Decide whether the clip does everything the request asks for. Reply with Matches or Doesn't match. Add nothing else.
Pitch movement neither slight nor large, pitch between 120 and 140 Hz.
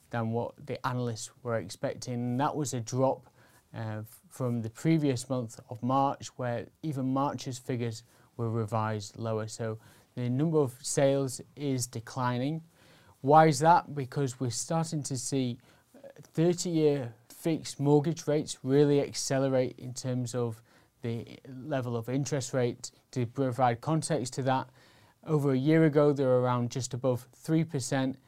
Matches